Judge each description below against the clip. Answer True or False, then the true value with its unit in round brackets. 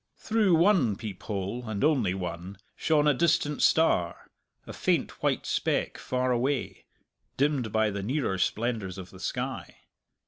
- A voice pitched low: True (120 Hz)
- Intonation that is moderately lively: False (7.2 semitones)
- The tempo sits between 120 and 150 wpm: True (145 wpm)